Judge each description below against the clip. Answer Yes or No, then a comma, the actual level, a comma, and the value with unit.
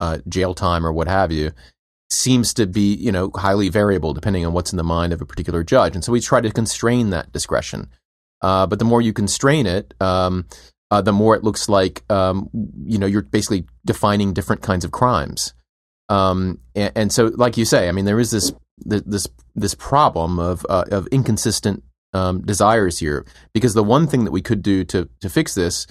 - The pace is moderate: No, fast, 210 wpm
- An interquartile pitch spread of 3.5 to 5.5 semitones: Yes, average, 4.1 semitones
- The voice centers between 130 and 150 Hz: No, very low, 95 Hz